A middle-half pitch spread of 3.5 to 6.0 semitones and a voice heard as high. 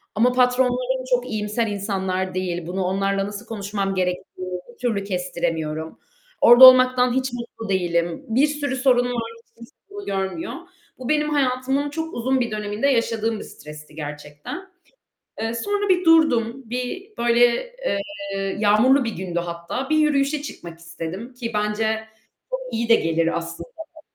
Yes: wide, 5.6 semitones; high, 230 Hz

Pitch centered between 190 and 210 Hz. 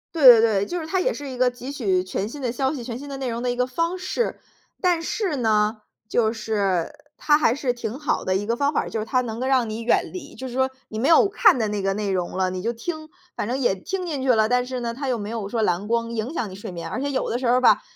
No: high, 245 Hz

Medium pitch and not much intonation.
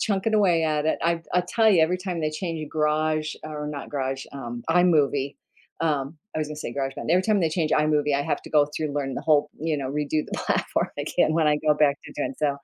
Yes: medium, 155 Hz; narrow, 2.2 semitones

